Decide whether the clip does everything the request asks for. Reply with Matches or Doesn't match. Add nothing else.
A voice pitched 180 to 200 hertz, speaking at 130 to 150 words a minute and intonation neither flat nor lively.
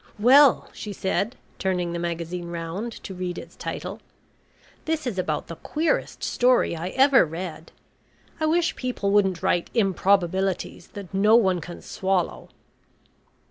Matches